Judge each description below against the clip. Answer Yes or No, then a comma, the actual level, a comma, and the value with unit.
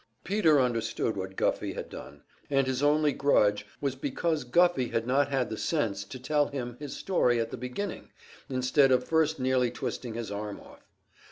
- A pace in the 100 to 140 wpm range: No, average, 180 wpm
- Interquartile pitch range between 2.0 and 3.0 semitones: No, average, 3.9 semitones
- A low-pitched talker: Yes, low, 130 Hz